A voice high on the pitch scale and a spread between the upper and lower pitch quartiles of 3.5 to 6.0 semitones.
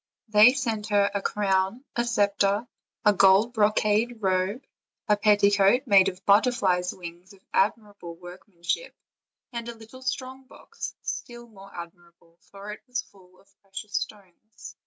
No: high, 205 Hz; average, 3.1 semitones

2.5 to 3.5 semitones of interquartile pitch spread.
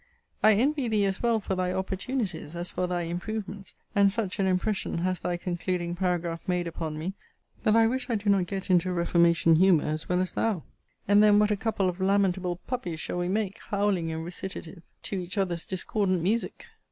Yes: average, 2.8 semitones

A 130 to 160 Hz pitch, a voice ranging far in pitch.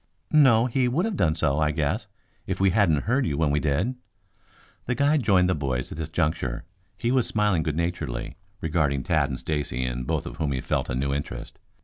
No: very low, 80 Hz; wide, 7.3 semitones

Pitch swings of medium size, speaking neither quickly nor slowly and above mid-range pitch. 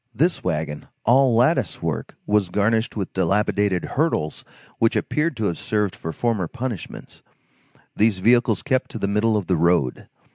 No: average, 4.6 semitones; average, 155 wpm; low, 105 Hz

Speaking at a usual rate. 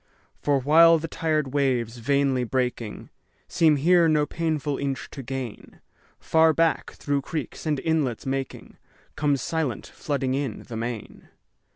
No: slow, 125 wpm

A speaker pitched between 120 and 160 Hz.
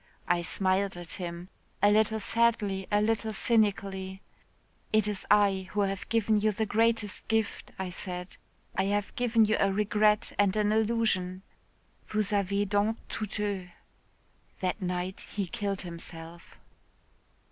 No: high, 205 Hz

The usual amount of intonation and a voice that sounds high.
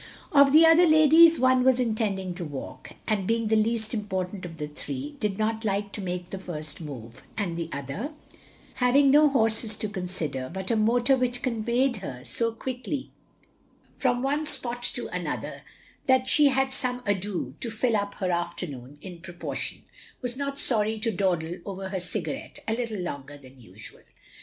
No: wide, 5.9 semitones; high, 215 Hz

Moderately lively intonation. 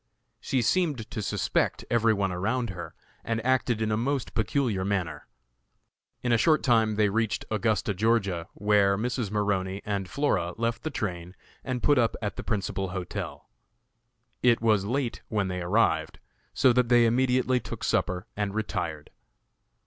Yes: average, 3.7 semitones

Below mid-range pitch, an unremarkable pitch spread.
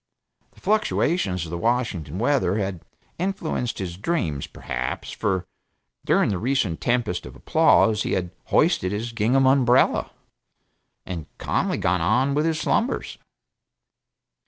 No: low, 110 Hz; wide, 6.9 semitones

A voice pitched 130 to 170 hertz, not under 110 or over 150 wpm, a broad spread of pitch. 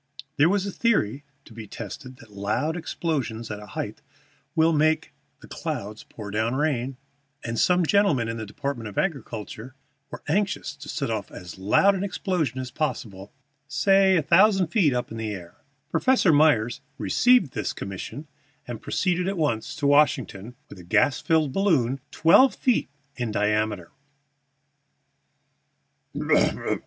Yes: low, 135 Hz; average, 145 wpm; wide, 7.6 semitones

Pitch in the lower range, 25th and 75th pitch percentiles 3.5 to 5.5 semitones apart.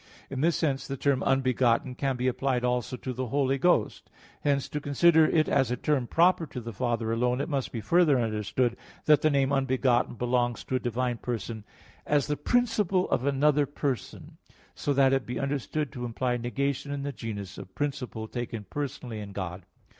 No: low, 130 Hz; average, 2.9 semitones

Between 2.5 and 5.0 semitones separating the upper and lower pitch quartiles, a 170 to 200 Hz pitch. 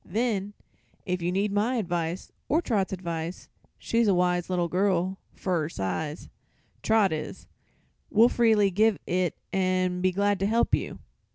Yes: average, 2.8 semitones; medium, 185 Hz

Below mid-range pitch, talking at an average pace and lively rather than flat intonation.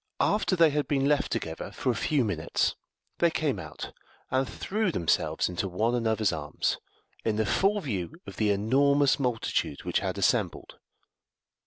Yes: low, 120 Hz; average, 160 wpm; wide, 6.2 semitones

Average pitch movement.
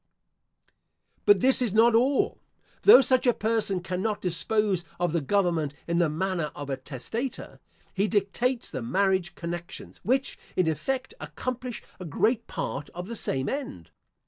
No: wide, 5.7 semitones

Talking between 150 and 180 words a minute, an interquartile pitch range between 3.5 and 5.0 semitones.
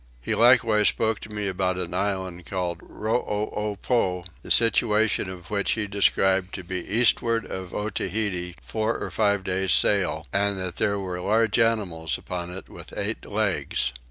No: average, 165 wpm; average, 2.9 semitones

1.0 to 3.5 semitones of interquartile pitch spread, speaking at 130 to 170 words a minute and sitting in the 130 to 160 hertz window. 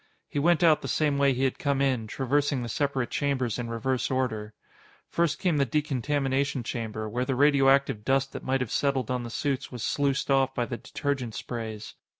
No: average, 2.7 semitones; average, 195 wpm; low, 135 Hz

